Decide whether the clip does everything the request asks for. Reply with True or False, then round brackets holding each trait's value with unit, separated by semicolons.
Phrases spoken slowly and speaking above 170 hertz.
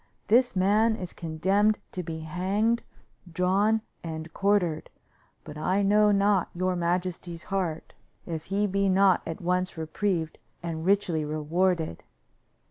True (130 wpm; 185 Hz)